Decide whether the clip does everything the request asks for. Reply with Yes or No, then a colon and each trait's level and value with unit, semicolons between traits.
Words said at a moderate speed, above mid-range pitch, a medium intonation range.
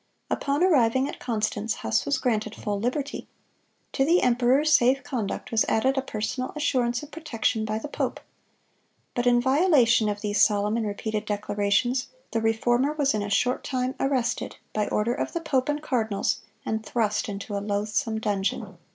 Yes: average, 170 wpm; high, 235 Hz; average, 4.0 semitones